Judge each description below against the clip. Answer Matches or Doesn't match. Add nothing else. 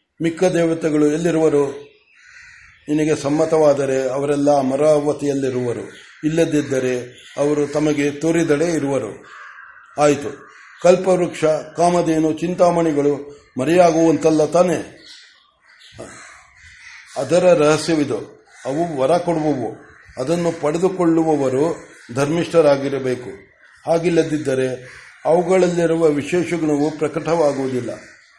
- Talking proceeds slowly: Matches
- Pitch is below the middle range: Doesn't match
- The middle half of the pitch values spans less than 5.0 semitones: Matches